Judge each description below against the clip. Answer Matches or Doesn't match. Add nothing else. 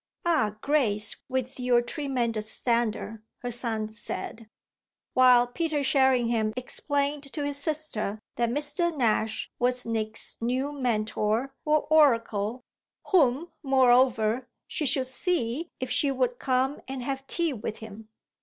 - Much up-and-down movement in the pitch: Doesn't match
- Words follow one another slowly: Matches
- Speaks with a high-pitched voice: Matches